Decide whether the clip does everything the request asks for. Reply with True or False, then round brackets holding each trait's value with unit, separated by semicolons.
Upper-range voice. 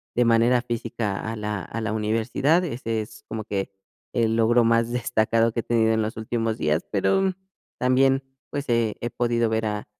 False (115 Hz)